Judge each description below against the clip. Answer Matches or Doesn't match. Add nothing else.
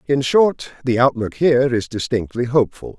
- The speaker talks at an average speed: Matches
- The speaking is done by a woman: Doesn't match